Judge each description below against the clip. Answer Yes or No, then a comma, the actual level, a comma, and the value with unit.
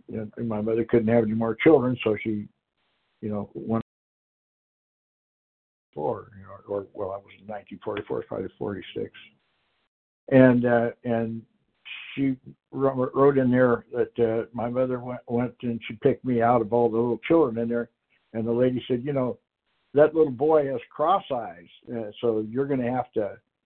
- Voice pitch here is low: Yes, low, 120 Hz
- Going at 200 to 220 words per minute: No, average, 180 wpm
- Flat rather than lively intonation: Yes, narrow, 2.0 semitones